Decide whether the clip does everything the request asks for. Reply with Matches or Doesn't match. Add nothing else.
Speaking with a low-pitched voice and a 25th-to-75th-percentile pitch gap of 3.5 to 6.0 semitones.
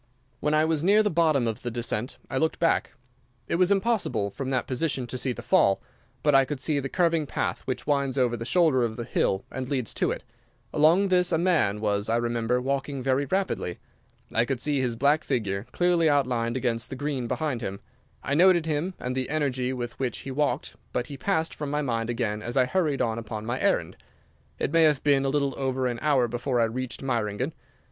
Matches